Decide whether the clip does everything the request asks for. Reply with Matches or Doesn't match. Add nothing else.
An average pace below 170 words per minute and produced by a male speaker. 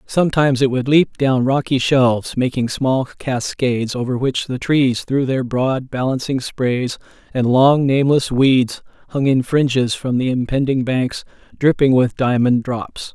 Matches